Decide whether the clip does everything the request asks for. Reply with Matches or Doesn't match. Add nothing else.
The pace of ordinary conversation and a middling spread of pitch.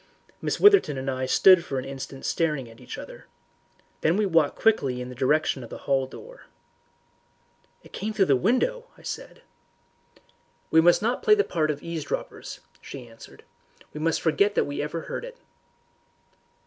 Doesn't match